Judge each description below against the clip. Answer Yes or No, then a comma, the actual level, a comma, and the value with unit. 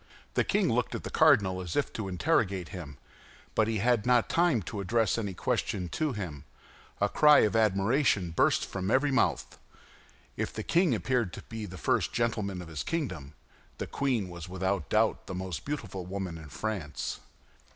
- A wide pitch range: No, average, 4.6 semitones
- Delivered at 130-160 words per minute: No, average, 175 wpm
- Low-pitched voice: Yes, low, 100 Hz